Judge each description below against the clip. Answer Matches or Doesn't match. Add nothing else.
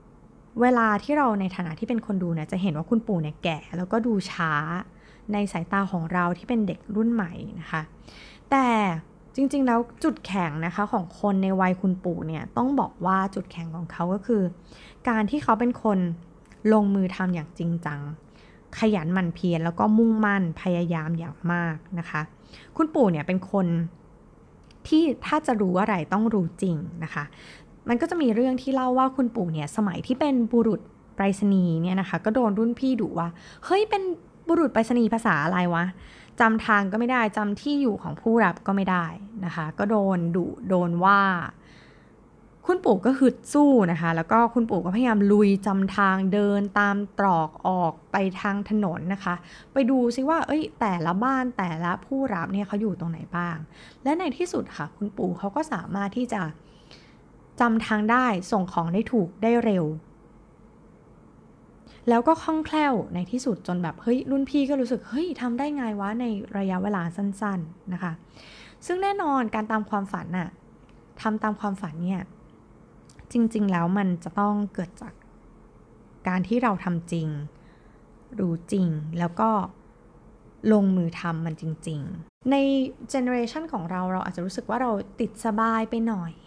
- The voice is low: Doesn't match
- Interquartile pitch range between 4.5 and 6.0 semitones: Matches